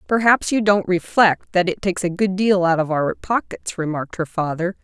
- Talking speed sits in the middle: No, fast, 210 wpm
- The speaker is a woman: Yes, female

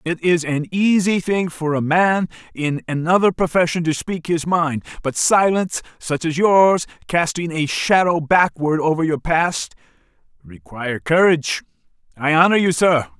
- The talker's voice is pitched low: No, medium, 165 Hz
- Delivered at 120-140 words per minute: No, average, 150 wpm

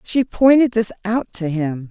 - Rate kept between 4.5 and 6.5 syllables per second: No, 4.2 syllables/s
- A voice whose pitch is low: No, high, 210 Hz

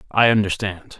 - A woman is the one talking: No, male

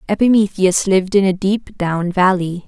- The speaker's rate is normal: Yes, average, 155 wpm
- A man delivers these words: No, female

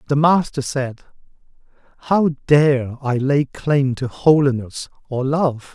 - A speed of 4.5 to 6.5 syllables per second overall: No, 3.6 syllables/s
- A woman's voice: No, male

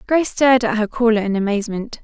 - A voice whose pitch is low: No, high, 225 Hz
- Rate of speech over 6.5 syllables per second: Yes, 7.0 syllables/s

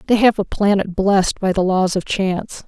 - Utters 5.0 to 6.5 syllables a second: Yes, 5.2 syllables/s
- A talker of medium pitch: No, high, 195 Hz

